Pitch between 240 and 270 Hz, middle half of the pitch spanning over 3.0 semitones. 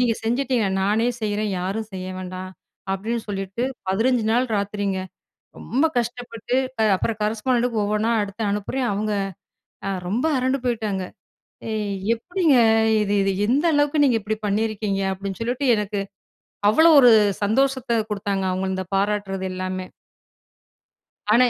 No: high, 215 Hz; average, 3.7 semitones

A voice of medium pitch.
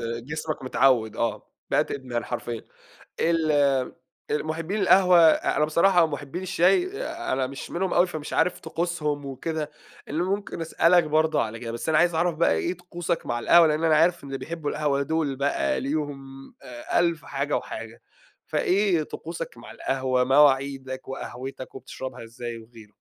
Yes: medium, 150 Hz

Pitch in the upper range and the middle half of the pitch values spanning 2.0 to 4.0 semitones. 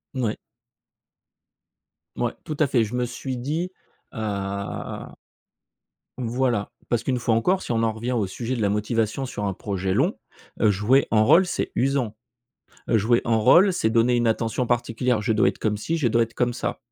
No: low, 115 Hz; average, 2.8 semitones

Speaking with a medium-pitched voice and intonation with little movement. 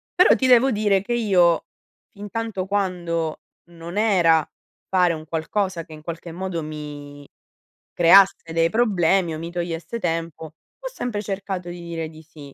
No: medium, 175 Hz; average, 3.5 semitones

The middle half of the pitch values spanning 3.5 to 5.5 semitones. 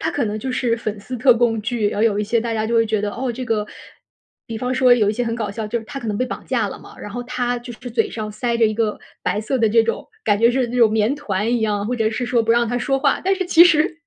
No: narrow, 2.4 semitones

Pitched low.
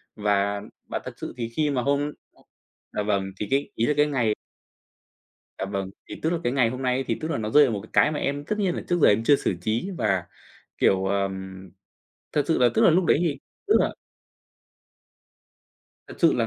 Yes: low, 120 Hz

